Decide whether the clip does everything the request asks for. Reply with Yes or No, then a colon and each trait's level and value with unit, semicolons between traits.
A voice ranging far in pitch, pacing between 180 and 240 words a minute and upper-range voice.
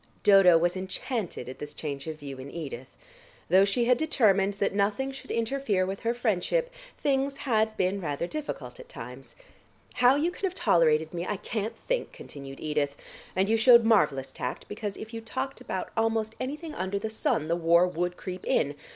Yes: wide, 6.1 semitones; average, 185 wpm; high, 200 Hz